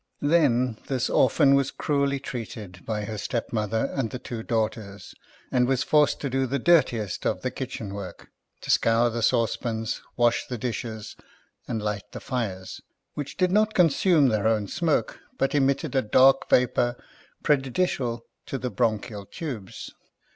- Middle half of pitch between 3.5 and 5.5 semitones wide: Yes, average, 3.9 semitones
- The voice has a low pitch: Yes, low, 120 Hz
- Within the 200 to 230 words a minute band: No, average, 155 wpm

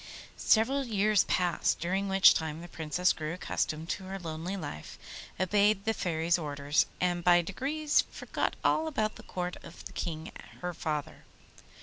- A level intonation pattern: No, average, 3.7 semitones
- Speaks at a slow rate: No, average, 155 wpm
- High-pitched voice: No, medium, 180 Hz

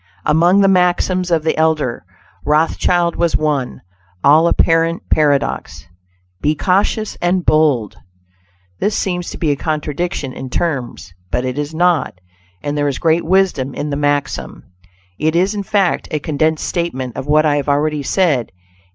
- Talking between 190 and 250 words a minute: No, average, 155 wpm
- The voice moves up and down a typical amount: Yes, average, 3.3 semitones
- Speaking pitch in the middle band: Yes, medium, 155 Hz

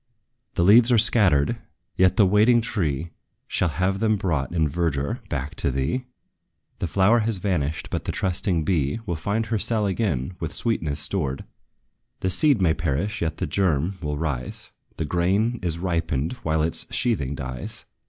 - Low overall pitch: Yes, very low, 85 Hz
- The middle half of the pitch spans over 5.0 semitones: Yes, wide, 5.4 semitones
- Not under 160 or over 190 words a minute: Yes, average, 165 wpm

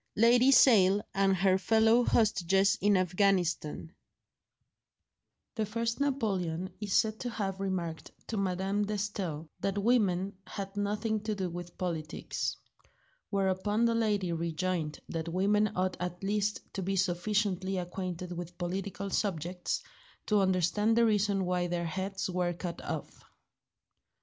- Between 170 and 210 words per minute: No, slow, 135 wpm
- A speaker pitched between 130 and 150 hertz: No, high, 195 Hz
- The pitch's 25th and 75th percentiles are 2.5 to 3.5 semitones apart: Yes, average, 2.8 semitones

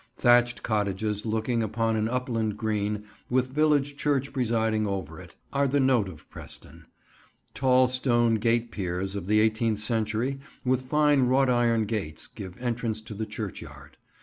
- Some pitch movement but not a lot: Yes, average, 3.2 semitones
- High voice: No, low, 115 Hz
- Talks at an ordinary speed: Yes, average, 150 wpm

